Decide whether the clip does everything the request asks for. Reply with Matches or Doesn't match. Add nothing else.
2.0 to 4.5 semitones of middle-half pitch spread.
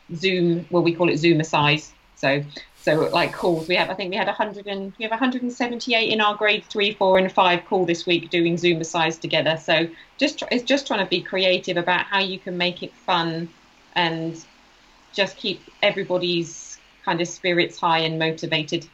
Matches